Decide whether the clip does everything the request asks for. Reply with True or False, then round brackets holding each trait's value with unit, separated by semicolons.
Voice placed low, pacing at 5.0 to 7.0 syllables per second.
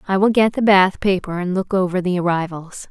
False (190 Hz; 5.5 syllables/s)